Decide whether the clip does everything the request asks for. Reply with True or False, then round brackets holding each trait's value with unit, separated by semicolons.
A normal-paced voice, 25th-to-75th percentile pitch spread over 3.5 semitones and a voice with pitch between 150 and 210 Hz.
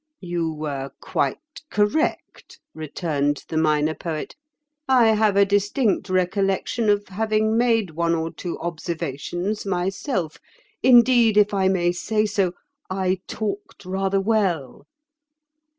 False (120 wpm; 4.1 semitones; 190 Hz)